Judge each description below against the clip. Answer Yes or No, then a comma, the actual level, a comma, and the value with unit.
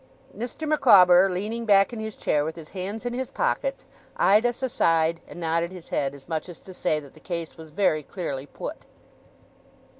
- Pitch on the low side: No, medium, 180 Hz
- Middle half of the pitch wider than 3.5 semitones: Yes, average, 5.2 semitones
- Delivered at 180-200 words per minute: Yes, average, 190 wpm